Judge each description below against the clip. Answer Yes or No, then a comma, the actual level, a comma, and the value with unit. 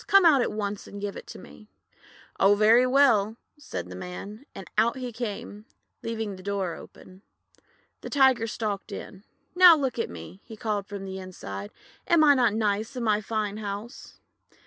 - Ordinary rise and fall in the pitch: Yes, average, 3.4 semitones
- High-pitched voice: Yes, high, 215 Hz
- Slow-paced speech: No, average, 175 wpm